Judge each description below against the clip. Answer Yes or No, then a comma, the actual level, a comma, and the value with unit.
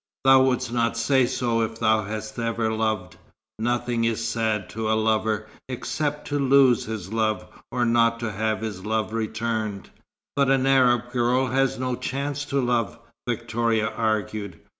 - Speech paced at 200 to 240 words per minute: No, average, 160 wpm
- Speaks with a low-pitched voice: Yes, low, 115 Hz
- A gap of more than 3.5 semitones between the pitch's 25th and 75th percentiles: No, narrow, 2.4 semitones